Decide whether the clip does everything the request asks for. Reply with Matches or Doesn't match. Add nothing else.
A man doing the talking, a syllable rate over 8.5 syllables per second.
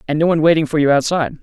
Matches